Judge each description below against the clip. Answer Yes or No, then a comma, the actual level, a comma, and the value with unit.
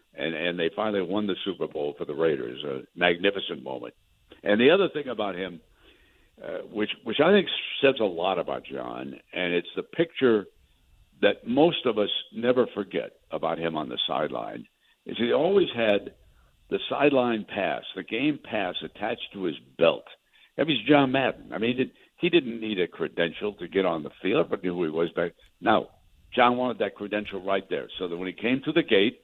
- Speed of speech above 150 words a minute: Yes, average, 200 wpm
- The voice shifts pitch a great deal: Yes, wide, 6.0 semitones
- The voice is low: Yes, low, 100 Hz